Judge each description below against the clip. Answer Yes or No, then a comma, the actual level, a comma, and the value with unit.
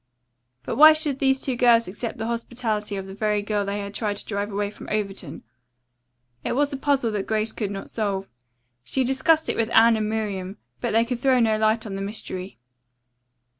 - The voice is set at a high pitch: Yes, high, 220 Hz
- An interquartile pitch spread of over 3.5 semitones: No, average, 3.1 semitones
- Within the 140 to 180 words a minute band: No, fast, 205 wpm